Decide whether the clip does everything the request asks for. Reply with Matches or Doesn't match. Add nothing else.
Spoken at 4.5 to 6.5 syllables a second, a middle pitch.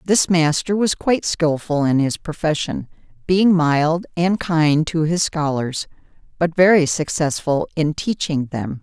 Doesn't match